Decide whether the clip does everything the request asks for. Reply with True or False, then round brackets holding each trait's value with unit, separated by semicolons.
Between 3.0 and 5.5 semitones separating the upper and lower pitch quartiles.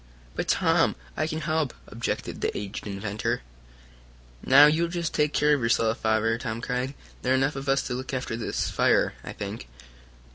True (4.8 semitones)